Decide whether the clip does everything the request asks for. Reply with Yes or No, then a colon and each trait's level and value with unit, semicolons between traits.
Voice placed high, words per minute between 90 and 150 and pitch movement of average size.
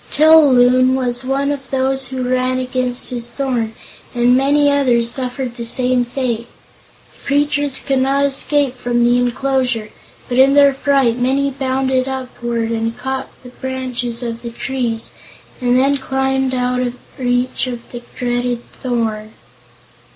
No: very high, 255 Hz; average, 145 wpm; narrow, 1.7 semitones